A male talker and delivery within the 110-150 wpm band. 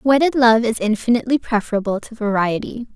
No: female; average, 140 wpm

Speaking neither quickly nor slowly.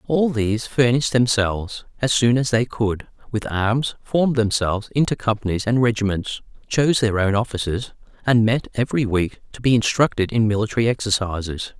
Yes: average, 160 wpm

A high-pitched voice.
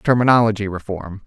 No: low, 105 Hz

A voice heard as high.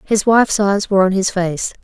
Yes: high, 195 Hz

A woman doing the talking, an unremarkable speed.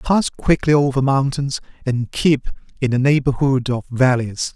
No: male; average, 145 wpm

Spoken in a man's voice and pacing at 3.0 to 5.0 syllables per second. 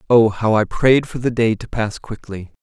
Yes: male; 4.7 syllables/s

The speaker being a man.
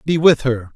Yes: male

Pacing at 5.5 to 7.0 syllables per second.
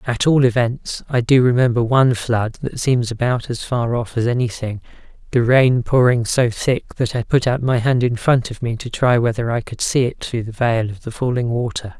No: 5.0 syllables/s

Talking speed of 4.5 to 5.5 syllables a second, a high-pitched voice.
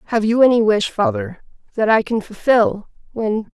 Yes: 4.9 syllables/s; high, 220 Hz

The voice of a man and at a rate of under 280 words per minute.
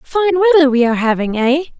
No: female; average, 200 wpm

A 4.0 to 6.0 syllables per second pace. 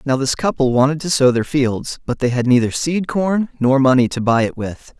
Yes: 5.1 syllables/s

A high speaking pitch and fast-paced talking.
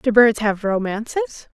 No: high, 215 Hz; average, 150 wpm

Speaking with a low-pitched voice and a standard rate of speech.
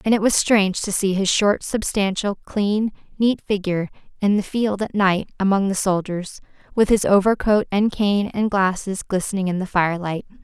No: high, 200 Hz; average, 180 wpm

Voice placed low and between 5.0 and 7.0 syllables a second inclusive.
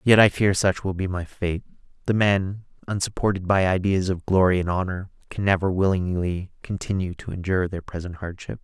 Yes: very low, 95 Hz; 5.4 syllables/s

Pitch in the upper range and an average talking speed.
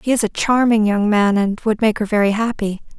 No: high, 215 Hz; fast, 240 wpm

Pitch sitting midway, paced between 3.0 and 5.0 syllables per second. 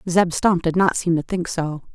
Yes: medium, 175 Hz; 4.6 syllables/s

